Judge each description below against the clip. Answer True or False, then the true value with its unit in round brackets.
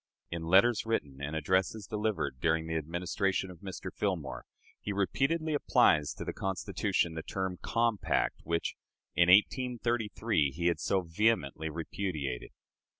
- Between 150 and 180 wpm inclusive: False (135 wpm)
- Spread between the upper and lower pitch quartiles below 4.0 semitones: False (4.9 semitones)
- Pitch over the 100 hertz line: False (95 Hz)